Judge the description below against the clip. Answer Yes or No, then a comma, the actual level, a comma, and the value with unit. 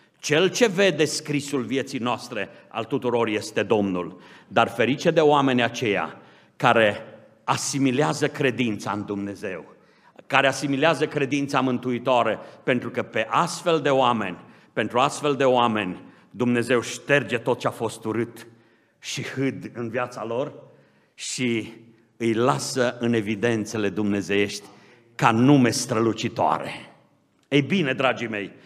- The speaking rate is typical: Yes, average, 125 wpm